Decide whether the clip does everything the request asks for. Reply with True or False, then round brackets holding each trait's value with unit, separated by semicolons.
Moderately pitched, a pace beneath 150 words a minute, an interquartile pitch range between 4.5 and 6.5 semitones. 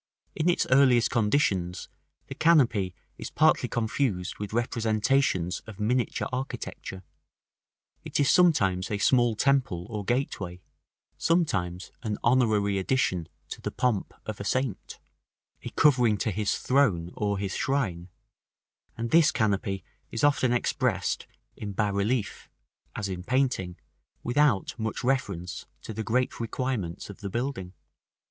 False (110 Hz; 135 wpm; 5.0 semitones)